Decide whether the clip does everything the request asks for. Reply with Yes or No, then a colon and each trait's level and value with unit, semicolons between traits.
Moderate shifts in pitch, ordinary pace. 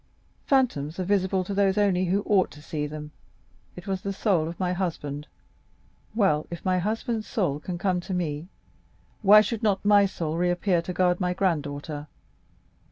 Yes: average, 3.5 semitones; average, 165 wpm